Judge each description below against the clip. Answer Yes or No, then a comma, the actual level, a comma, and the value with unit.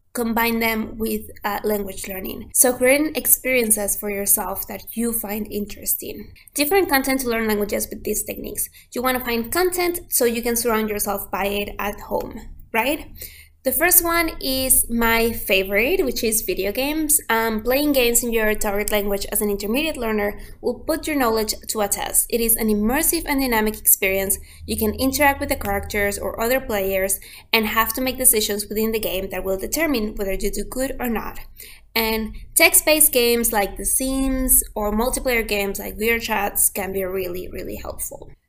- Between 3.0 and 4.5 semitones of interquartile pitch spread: Yes, average, 3.9 semitones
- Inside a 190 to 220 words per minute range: No, average, 180 wpm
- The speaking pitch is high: Yes, high, 225 Hz